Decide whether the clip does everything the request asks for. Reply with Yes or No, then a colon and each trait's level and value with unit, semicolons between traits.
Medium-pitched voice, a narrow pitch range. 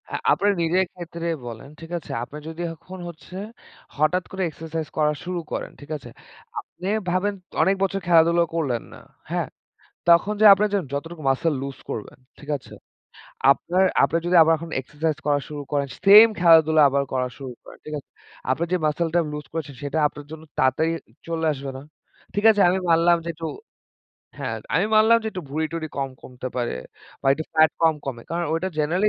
No: medium, 160 Hz; average, 3.1 semitones